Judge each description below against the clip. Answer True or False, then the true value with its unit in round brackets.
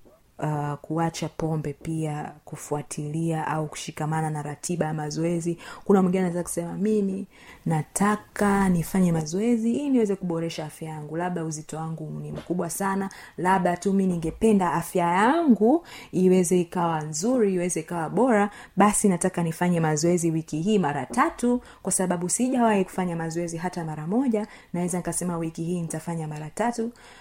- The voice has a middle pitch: True (175 Hz)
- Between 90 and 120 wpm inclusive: False (135 wpm)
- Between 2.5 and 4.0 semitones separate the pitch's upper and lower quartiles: True (3.6 semitones)